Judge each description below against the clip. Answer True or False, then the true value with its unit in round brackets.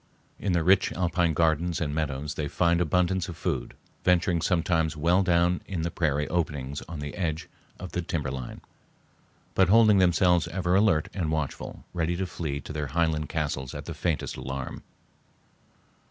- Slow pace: False (165 wpm)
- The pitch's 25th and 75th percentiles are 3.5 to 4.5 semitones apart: False (2.8 semitones)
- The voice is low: True (85 Hz)